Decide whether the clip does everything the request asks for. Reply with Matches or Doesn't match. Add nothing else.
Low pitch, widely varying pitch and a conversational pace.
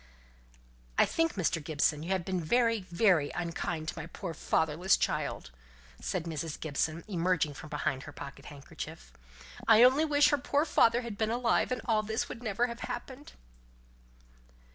Doesn't match